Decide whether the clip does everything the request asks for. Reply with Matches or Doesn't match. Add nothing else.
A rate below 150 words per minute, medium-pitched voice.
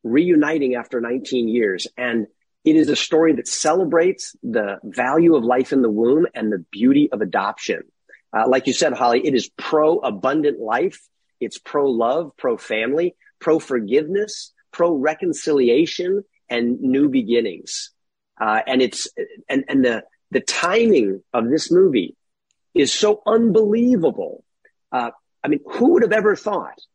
Matches